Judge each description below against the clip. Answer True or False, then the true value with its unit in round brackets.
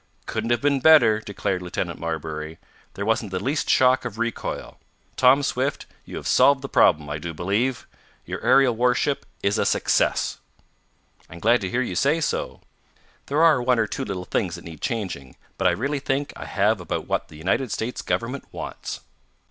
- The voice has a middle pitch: False (115 Hz)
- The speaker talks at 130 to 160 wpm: False (185 wpm)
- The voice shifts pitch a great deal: True (6.4 semitones)